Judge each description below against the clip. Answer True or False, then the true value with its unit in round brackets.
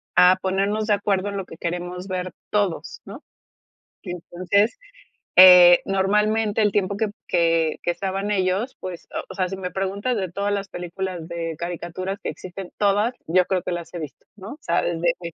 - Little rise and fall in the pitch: True (2.3 semitones)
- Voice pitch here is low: False (185 Hz)